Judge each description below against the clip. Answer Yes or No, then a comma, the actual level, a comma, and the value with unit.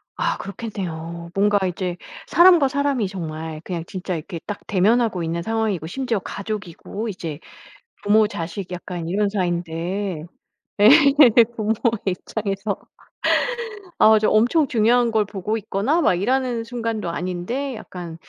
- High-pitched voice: Yes, high, 200 Hz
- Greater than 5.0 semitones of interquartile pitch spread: No, average, 4.3 semitones